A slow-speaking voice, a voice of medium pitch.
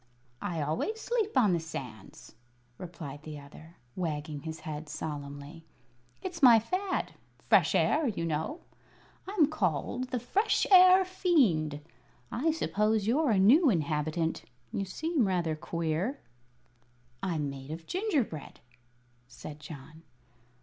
Yes: slow, 120 wpm; medium, 175 Hz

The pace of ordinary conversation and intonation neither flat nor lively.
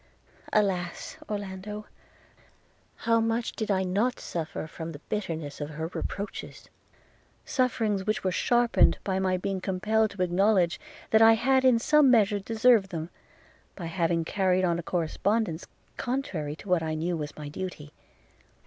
Yes: average, 150 wpm; average, 4.5 semitones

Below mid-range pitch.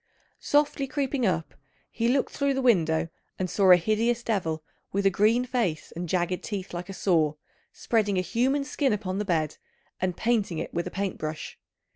No: high, 200 Hz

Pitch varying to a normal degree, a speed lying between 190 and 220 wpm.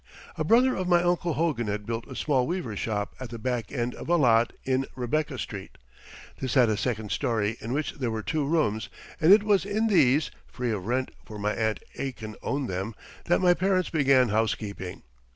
No: wide, 6.4 semitones; fast, 205 wpm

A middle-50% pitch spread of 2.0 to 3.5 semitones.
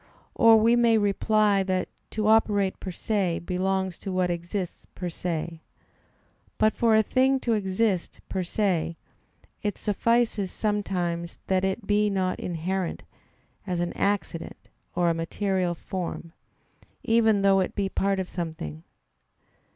Yes: average, 3.0 semitones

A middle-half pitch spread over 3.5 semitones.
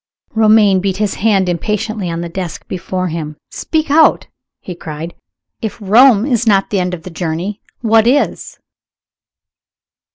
Yes: average, 4.0 semitones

